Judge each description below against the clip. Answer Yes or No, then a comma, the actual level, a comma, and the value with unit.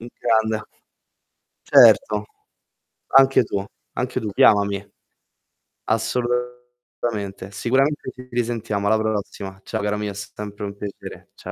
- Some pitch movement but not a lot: Yes, average, 3.3 semitones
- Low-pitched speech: Yes, low, 110 Hz